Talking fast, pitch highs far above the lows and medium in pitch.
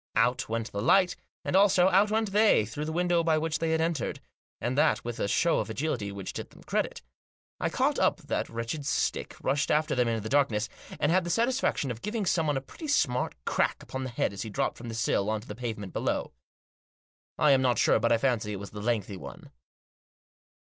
No: fast, 225 wpm; wide, 6.7 semitones; low, 130 Hz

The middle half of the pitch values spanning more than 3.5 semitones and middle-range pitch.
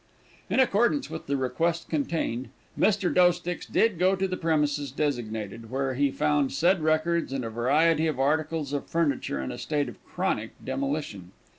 Yes: average, 4.2 semitones; medium, 150 Hz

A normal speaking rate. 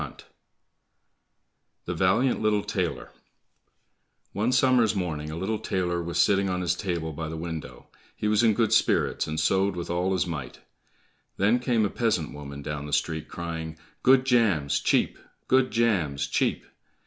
Yes: average, 160 wpm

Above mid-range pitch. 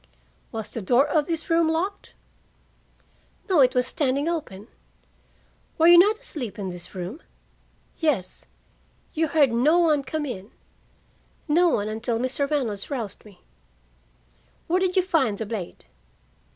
Yes: very high, 275 Hz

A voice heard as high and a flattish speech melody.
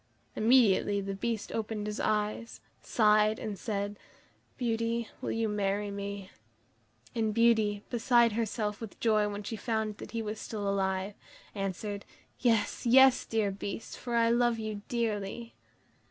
Yes: high, 215 Hz; narrow, 2.1 semitones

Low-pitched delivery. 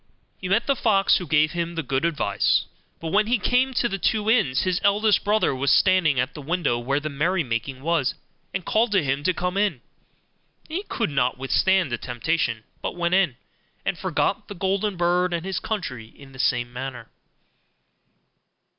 No: medium, 170 Hz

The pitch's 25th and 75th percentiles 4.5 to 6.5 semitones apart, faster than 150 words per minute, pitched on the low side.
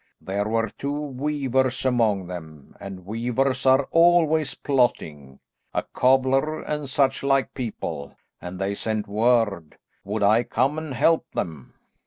No: wide, 5.4 semitones; slow, 135 wpm; low, 125 Hz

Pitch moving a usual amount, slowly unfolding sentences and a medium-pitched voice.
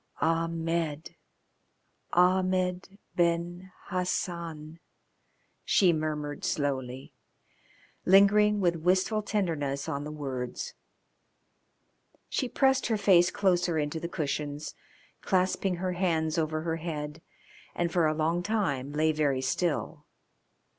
Yes: average, 3.3 semitones; slow, 105 wpm; medium, 165 Hz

